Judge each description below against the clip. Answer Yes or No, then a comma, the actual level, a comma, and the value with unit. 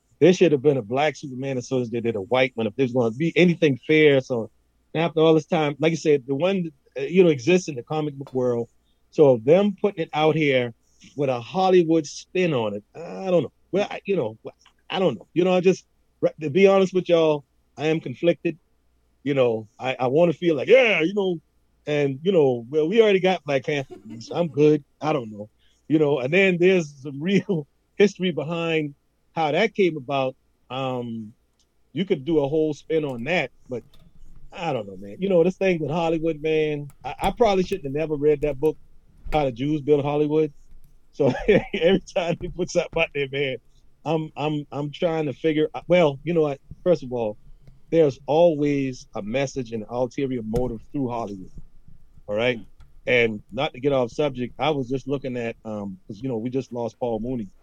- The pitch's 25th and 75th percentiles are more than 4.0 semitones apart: Yes, average, 4.4 semitones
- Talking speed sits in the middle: No, fast, 210 wpm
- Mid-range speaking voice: Yes, medium, 150 Hz